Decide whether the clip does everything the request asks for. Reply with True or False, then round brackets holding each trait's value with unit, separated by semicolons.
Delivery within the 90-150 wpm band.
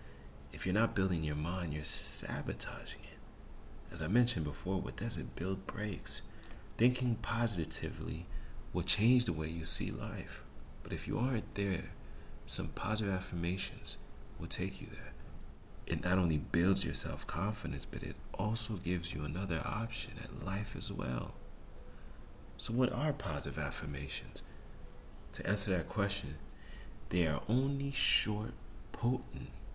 True (140 wpm)